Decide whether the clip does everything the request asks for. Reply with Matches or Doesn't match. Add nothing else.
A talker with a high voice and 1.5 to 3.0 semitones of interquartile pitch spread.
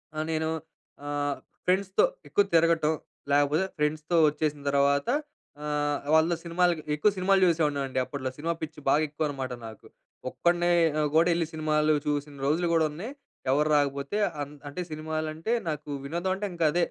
Doesn't match